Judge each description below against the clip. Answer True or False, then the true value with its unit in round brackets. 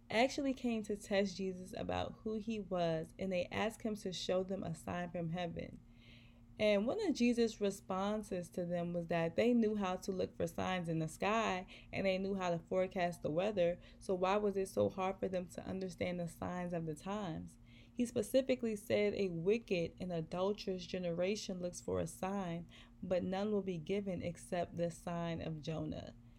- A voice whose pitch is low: False (185 Hz)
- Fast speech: False (190 wpm)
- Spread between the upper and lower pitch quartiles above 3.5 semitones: False (3.1 semitones)